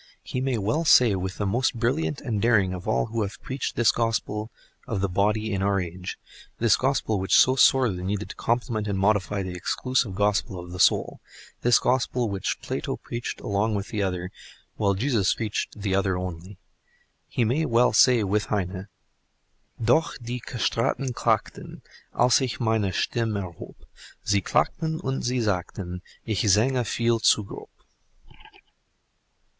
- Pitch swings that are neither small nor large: Yes, average, 3.7 semitones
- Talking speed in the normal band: Yes, average, 160 wpm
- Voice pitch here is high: No, low, 110 Hz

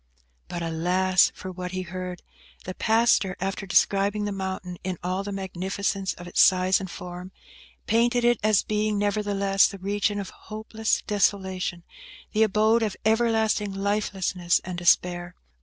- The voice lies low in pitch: No, high, 195 Hz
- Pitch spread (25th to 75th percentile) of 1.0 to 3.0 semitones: Yes, narrow, 2.4 semitones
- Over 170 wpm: No, average, 145 wpm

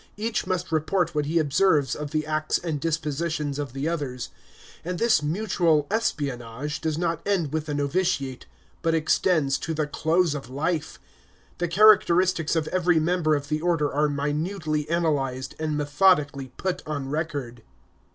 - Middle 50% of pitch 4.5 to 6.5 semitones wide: No, average, 2.9 semitones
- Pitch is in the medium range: Yes, medium, 155 Hz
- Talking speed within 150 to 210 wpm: Yes, average, 155 wpm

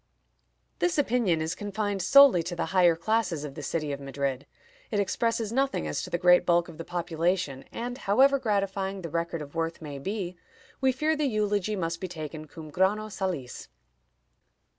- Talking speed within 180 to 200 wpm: Yes, average, 185 wpm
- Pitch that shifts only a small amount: No, average, 4.7 semitones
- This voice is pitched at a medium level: Yes, medium, 180 Hz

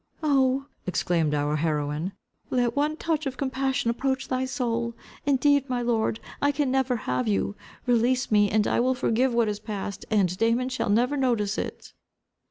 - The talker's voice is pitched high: Yes, high, 240 Hz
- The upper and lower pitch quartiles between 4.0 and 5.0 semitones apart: Yes, average, 4.3 semitones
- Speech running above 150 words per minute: Yes, average, 170 wpm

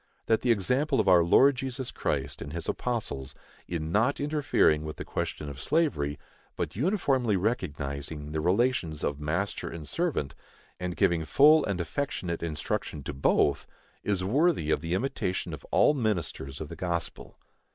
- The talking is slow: No, average, 160 wpm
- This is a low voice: Yes, very low, 90 Hz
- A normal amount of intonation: No, wide, 8.7 semitones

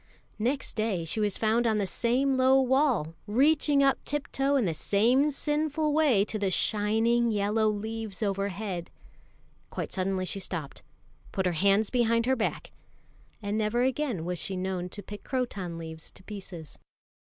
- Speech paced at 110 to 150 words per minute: No, average, 160 wpm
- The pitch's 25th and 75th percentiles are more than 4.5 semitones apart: Yes, average, 5.0 semitones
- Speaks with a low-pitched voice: No, high, 215 Hz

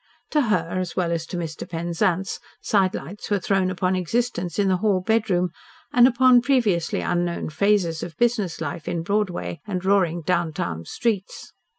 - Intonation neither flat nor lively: Yes, average, 3.4 semitones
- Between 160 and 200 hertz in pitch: Yes, medium, 185 Hz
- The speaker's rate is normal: Yes, average, 160 wpm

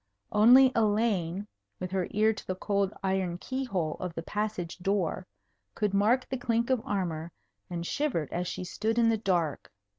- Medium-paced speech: Yes, average, 175 wpm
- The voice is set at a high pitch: Yes, high, 200 Hz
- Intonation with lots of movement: No, average, 3.9 semitones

